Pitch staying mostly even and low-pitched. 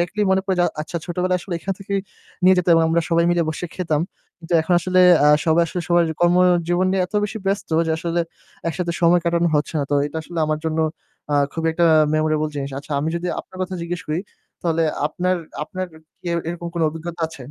No: narrow, 1.9 semitones; medium, 170 Hz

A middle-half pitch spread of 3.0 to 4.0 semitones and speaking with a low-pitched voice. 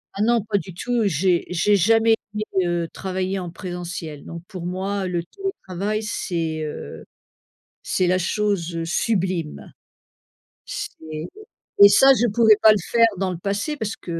No: average, 3.5 semitones; high, 190 Hz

